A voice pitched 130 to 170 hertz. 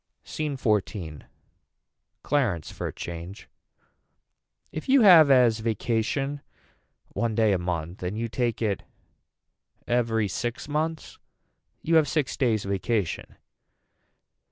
No: low, 115 Hz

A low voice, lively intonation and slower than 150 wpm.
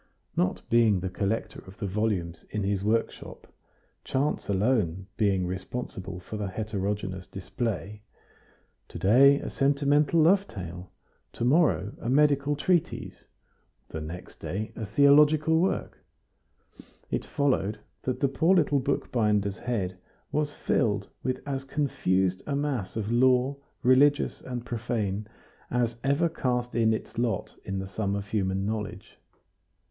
Yes: low, 115 Hz; wide, 6.1 semitones; slow, 135 wpm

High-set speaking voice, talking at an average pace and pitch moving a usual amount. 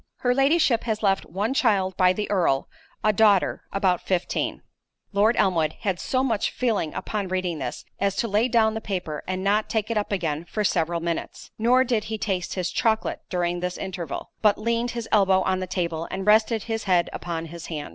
Yes: high, 195 Hz; average, 195 wpm; average, 3.6 semitones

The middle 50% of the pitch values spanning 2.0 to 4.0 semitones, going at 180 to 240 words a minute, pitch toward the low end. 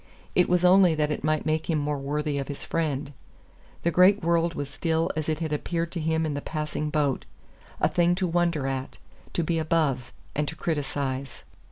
No: narrow, 2.6 semitones; average, 200 wpm; medium, 155 Hz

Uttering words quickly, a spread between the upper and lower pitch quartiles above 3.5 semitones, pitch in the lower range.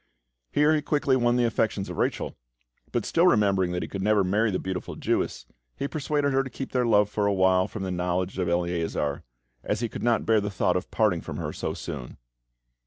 Yes: fast, 215 wpm; average, 4.9 semitones; low, 105 Hz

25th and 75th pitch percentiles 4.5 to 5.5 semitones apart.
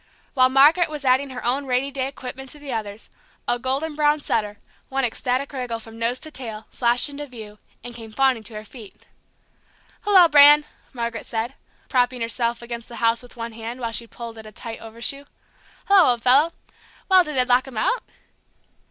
No: average, 3.3 semitones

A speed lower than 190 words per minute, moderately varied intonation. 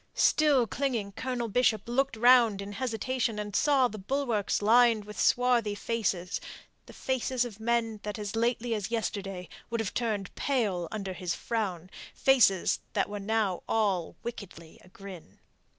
Yes: average, 150 wpm; average, 3.4 semitones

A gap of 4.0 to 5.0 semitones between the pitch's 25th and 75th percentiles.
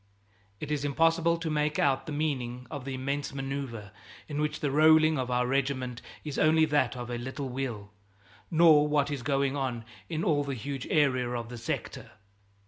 No: average, 3.0 semitones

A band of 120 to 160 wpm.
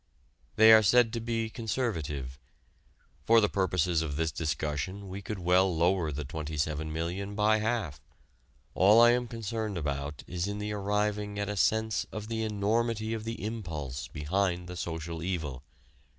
Yes: average, 150 wpm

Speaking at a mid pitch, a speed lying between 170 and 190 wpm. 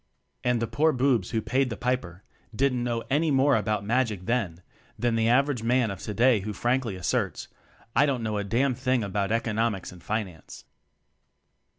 No: low, 115 Hz; average, 180 wpm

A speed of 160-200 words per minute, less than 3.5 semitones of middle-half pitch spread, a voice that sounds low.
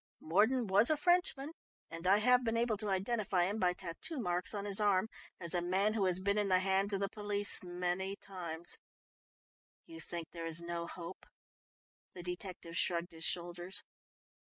No: average, 175 wpm; average, 3.0 semitones; high, 190 Hz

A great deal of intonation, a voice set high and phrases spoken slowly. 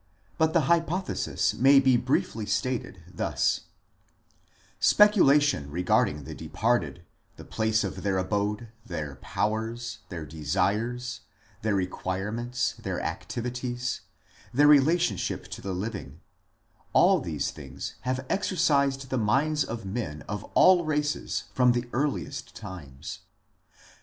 No: wide, 5.8 semitones; low, 120 Hz; slow, 115 wpm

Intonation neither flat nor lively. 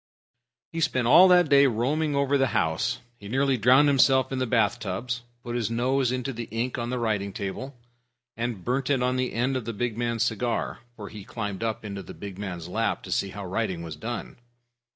Yes: average, 3.9 semitones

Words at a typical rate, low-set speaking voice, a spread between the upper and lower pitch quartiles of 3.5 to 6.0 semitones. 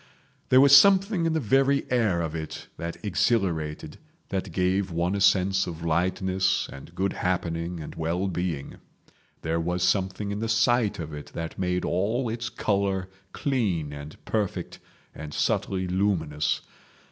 Yes: average, 150 wpm; very low, 95 Hz; average, 4.1 semitones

